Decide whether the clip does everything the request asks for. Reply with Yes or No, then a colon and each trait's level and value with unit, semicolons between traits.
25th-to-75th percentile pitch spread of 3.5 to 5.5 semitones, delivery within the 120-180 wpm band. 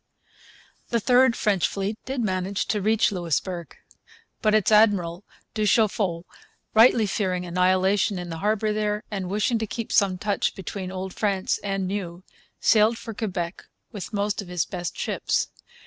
No: average, 2.7 semitones; average, 155 wpm